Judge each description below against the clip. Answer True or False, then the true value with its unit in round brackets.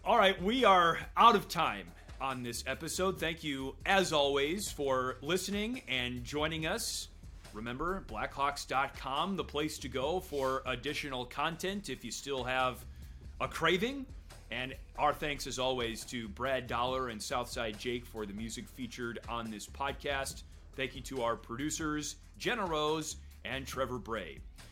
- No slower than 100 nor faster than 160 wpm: True (150 wpm)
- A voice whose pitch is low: True (130 Hz)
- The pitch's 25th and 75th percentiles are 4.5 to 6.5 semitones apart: True (5.0 semitones)